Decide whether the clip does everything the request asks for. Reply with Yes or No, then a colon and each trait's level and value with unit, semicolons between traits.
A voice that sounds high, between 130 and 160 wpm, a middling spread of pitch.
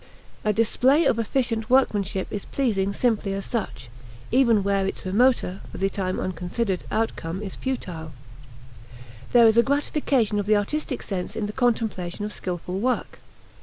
Yes: high, 210 Hz; average, 155 wpm; average, 4.0 semitones